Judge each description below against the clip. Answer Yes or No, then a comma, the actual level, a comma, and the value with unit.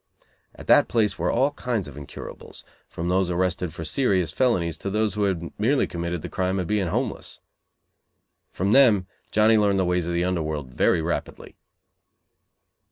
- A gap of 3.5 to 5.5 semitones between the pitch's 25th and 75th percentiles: Yes, average, 3.8 semitones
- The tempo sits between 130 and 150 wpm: No, average, 170 wpm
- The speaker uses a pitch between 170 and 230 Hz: No, very low, 95 Hz